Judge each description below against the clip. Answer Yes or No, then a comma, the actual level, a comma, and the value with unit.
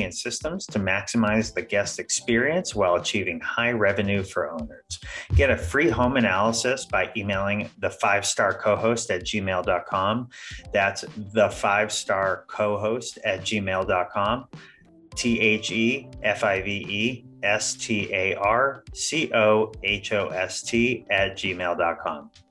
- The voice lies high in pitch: No, low, 105 Hz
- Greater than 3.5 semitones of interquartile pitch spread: No, average, 3.0 semitones